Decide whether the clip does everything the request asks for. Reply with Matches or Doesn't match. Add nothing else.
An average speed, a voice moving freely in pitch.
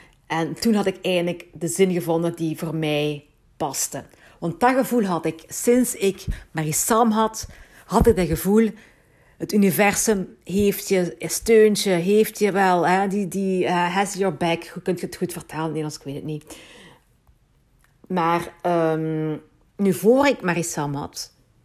Doesn't match